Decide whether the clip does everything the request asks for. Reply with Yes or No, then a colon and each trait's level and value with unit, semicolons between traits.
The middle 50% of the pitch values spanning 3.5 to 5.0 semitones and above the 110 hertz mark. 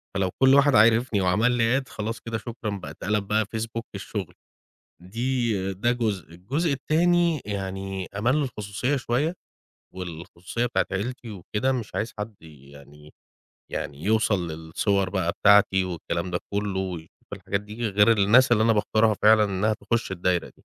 No: average, 3.8 semitones; low, 105 Hz